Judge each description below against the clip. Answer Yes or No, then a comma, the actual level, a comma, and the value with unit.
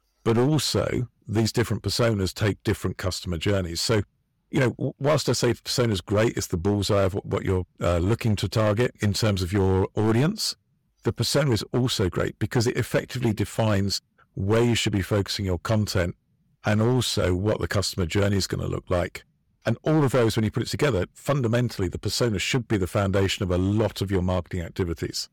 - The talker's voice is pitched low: Yes, low, 110 Hz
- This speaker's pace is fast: No, average, 195 wpm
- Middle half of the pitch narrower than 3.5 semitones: No, average, 3.8 semitones